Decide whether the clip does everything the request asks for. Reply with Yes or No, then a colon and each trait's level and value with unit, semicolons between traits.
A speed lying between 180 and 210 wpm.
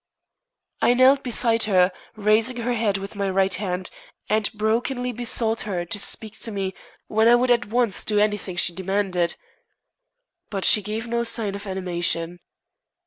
No: average, 160 wpm